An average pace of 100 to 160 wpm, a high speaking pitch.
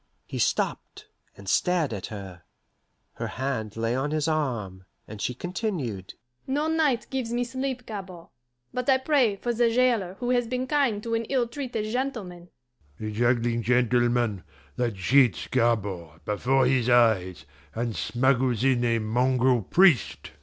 No: average, 150 wpm; low, 130 Hz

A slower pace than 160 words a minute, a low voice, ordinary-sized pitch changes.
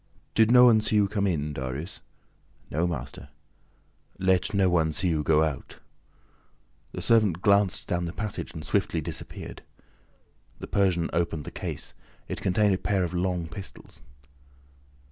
Yes: average, 150 wpm; very low, 90 Hz; average, 4.0 semitones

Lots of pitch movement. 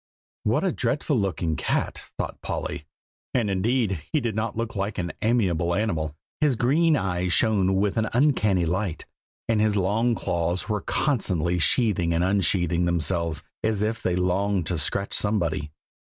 No: average, 4.2 semitones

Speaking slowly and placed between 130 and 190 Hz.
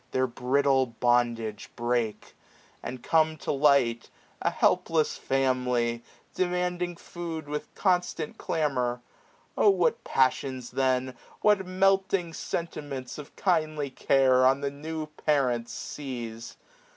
Yes: slow, 115 wpm; medium, 140 Hz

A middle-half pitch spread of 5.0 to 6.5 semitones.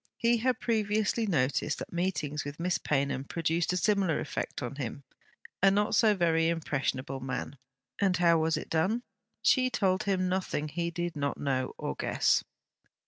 Yes: average, 5.3 semitones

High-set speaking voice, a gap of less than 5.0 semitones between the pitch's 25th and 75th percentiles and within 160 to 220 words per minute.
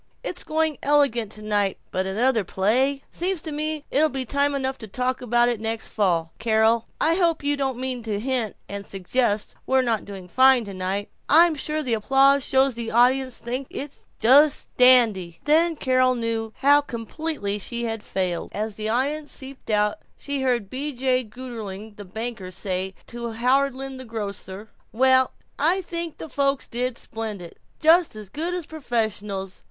Yes: high, 245 Hz; average, 4.5 semitones; average, 170 wpm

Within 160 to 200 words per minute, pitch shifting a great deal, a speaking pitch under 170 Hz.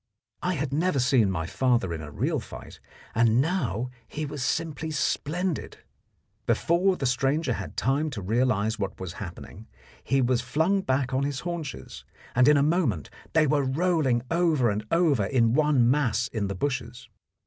No: average, 170 wpm; average, 4.9 semitones; low, 135 Hz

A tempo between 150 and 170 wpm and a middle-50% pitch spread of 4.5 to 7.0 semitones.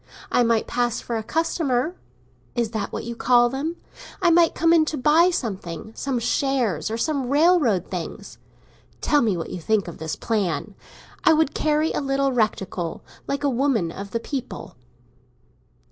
Yes: average, 160 wpm; wide, 5.6 semitones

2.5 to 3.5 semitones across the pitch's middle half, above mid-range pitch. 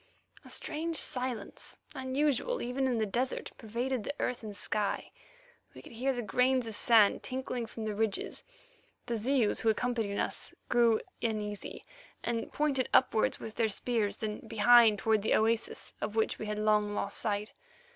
Yes: average, 2.9 semitones; high, 230 Hz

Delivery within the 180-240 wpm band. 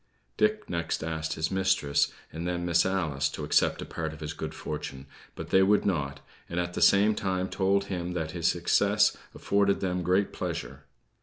Yes: average, 185 wpm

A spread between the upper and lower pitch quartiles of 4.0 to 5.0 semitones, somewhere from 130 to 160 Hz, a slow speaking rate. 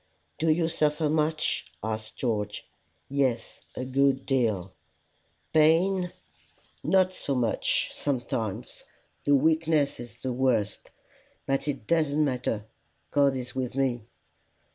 Yes: average, 4.3 semitones; low, 135 Hz; slow, 115 wpm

